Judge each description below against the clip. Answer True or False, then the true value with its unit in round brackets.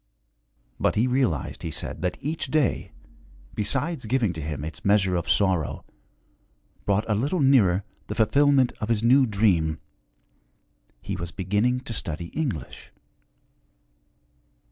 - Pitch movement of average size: False (6.7 semitones)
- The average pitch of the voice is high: False (105 Hz)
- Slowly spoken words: True (130 wpm)